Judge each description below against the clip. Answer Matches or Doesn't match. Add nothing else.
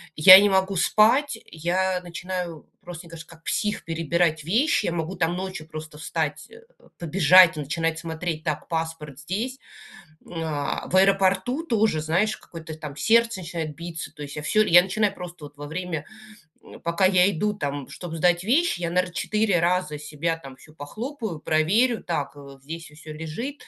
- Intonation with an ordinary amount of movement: Matches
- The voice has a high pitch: Doesn't match